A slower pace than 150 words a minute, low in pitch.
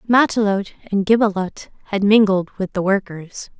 No: slow, 135 wpm; high, 200 Hz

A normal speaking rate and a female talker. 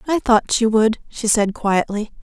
Yes: average, 190 wpm; female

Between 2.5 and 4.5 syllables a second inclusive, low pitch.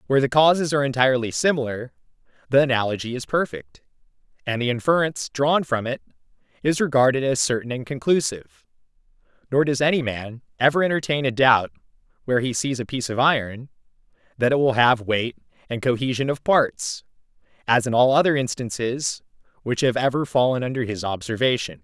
No: 5.9 syllables/s; low, 125 Hz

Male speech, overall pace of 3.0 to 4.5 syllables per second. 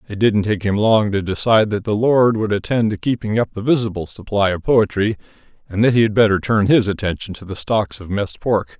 No: male; 5.6 syllables/s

